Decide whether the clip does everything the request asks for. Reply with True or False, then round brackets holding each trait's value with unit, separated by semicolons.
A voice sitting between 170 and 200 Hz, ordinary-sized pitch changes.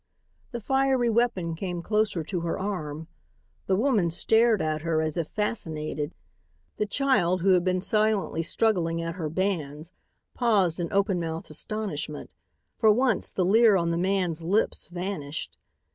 True (185 Hz; 4.5 semitones)